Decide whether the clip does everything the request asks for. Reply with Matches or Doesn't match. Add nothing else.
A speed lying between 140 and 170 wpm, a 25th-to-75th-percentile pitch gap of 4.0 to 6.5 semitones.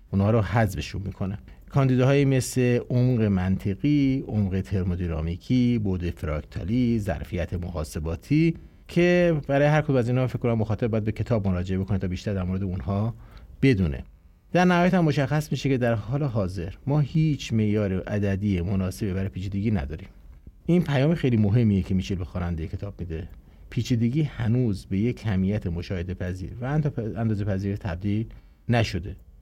Matches